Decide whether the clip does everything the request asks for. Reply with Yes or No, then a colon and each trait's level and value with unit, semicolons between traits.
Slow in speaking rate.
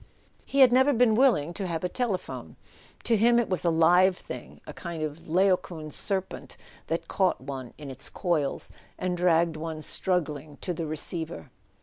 No: average, 175 wpm